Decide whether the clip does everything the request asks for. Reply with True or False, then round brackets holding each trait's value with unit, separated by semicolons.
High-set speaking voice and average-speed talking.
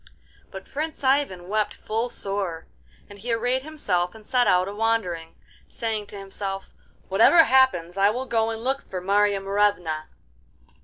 True (205 Hz; 155 wpm)